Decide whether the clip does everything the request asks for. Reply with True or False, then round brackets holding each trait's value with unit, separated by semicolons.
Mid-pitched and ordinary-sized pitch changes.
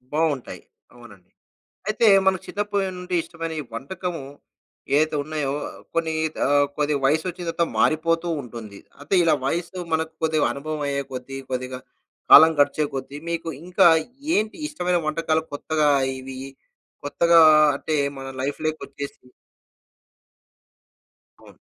True (155 Hz; 3.3 semitones)